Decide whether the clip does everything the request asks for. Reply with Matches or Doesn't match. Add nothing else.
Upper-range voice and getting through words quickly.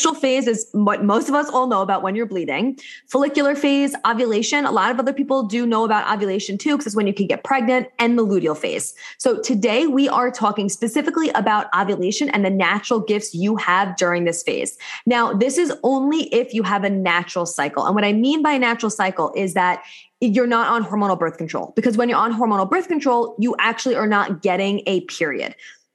Matches